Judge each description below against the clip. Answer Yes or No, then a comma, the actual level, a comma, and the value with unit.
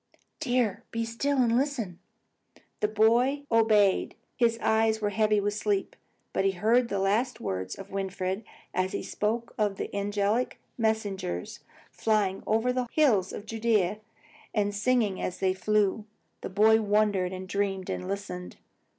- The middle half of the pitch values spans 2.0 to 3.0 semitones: Yes, average, 2.7 semitones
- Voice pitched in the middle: No, high, 210 Hz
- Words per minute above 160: No, average, 150 wpm